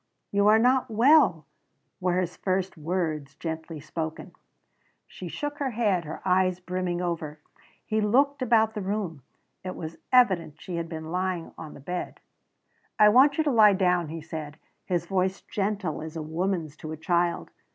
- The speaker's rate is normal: Yes, average, 170 wpm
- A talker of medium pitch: Yes, medium, 180 Hz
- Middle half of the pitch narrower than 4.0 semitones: No, average, 4.5 semitones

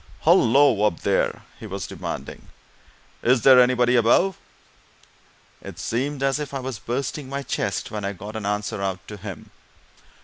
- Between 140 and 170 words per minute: Yes, average, 160 wpm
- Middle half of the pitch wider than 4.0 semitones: Yes, average, 4.7 semitones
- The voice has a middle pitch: No, low, 120 Hz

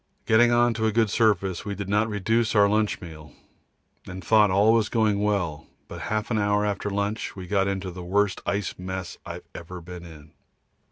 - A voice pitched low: Yes, low, 100 Hz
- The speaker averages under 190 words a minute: No, average, 200 wpm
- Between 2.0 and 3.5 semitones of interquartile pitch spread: Yes, average, 2.8 semitones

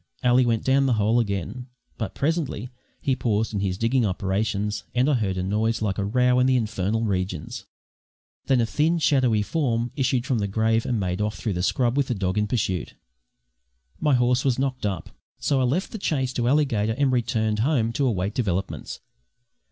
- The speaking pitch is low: Yes, low, 115 Hz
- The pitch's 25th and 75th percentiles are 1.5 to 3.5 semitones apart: No, average, 3.9 semitones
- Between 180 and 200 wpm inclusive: Yes, average, 195 wpm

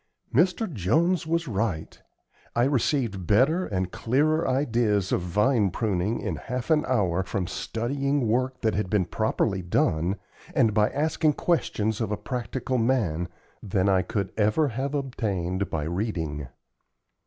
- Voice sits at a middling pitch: No, low, 110 Hz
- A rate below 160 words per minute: Yes, average, 145 wpm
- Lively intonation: Yes, wide, 6.0 semitones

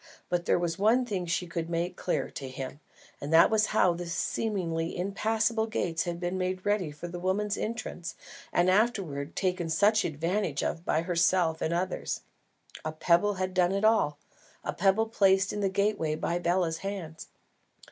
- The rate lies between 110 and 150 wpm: No, average, 175 wpm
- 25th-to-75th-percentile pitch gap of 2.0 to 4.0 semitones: Yes, average, 3.3 semitones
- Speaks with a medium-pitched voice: Yes, medium, 180 Hz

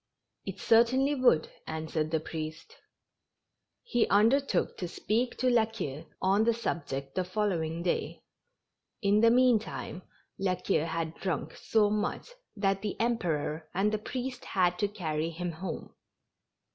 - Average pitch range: No, wide, 5.7 semitones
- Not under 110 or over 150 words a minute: Yes, average, 145 wpm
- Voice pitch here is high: Yes, high, 195 Hz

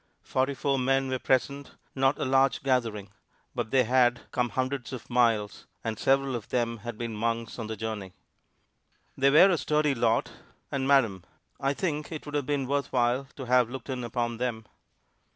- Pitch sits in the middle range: No, low, 125 Hz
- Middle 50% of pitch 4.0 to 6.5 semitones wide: No, average, 2.8 semitones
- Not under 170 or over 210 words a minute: Yes, average, 185 wpm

